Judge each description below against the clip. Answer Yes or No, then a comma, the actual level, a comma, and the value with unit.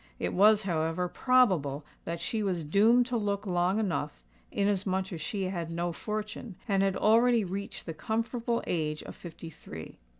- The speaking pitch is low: No, high, 195 Hz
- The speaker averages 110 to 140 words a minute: No, average, 165 wpm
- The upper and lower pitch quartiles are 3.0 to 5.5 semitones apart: Yes, average, 4.2 semitones